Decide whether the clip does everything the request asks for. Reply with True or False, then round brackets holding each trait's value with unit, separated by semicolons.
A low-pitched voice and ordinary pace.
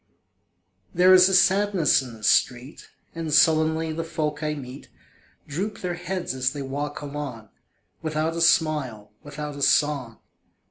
False (150 Hz; 145 wpm)